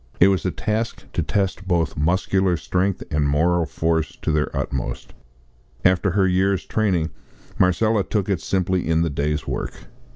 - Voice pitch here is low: Yes, very low, 90 Hz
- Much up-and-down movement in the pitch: No, average, 3.2 semitones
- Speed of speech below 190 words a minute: Yes, average, 160 wpm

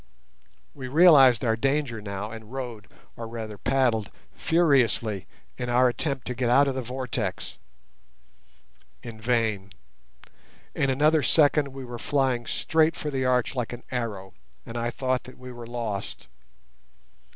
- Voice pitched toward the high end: No, low, 125 Hz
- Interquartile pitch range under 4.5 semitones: Yes, average, 2.9 semitones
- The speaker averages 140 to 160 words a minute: Yes, average, 145 wpm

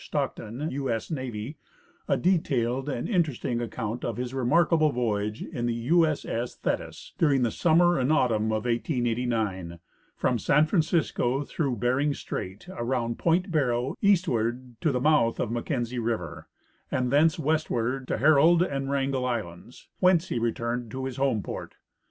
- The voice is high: No, low, 125 Hz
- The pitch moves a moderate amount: Yes, average, 4.5 semitones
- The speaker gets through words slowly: No, average, 155 wpm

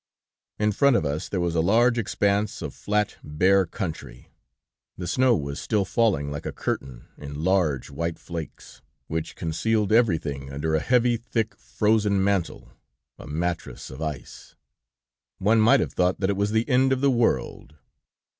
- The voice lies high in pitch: No, very low, 95 Hz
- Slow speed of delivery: No, average, 165 wpm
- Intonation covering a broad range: Yes, wide, 6.1 semitones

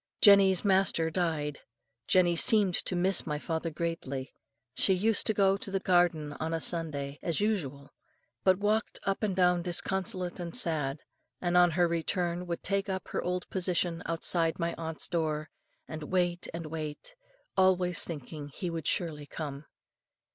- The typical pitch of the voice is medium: Yes, medium, 175 Hz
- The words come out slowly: No, average, 160 wpm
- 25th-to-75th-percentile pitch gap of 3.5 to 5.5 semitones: No, average, 2.9 semitones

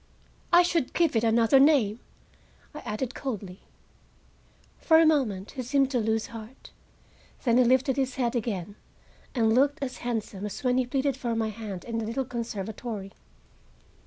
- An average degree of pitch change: Yes, average, 3.5 semitones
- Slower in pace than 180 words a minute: Yes, average, 160 wpm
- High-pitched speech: Yes, high, 240 Hz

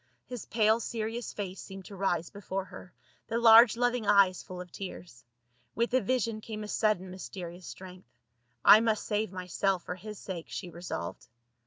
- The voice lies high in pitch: Yes, high, 200 Hz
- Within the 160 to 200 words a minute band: Yes, average, 175 wpm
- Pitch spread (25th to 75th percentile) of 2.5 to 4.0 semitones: Yes, average, 3.3 semitones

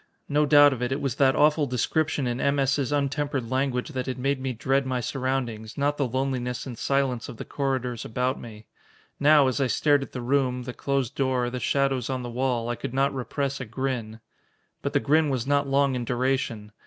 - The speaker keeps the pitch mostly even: Yes, narrow, 2.1 semitones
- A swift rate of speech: Yes, fast, 215 wpm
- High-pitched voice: No, low, 130 Hz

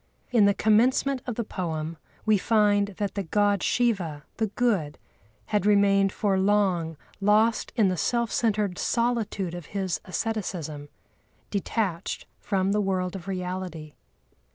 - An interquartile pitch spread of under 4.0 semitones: Yes, average, 2.9 semitones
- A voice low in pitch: No, high, 200 Hz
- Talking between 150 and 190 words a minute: No, slow, 135 wpm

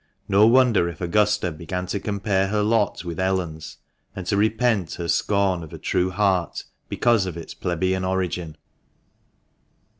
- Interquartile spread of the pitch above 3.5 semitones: No, average, 3.0 semitones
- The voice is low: Yes, very low, 95 Hz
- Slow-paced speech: No, average, 150 wpm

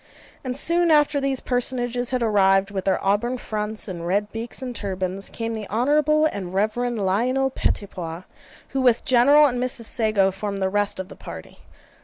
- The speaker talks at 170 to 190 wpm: Yes, average, 175 wpm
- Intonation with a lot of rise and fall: No, average, 4.5 semitones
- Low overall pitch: No, high, 225 Hz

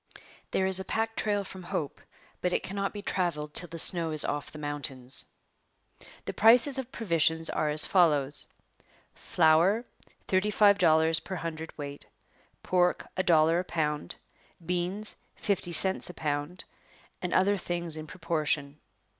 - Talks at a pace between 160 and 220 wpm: No, average, 150 wpm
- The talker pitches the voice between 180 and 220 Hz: No, medium, 170 Hz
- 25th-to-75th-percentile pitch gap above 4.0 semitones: No, average, 3.7 semitones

